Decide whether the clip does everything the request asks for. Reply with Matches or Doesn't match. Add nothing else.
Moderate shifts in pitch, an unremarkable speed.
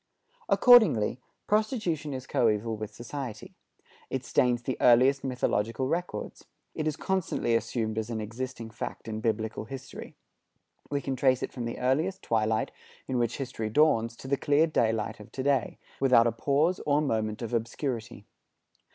Matches